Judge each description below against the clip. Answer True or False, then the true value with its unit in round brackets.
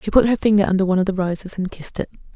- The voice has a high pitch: True (195 Hz)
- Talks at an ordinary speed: False (305 wpm)